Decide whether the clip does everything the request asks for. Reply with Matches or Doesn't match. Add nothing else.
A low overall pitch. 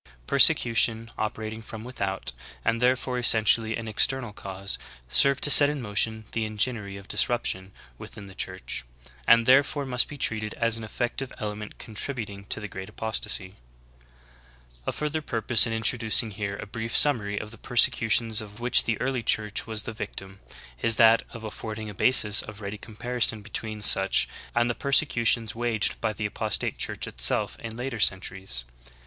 Matches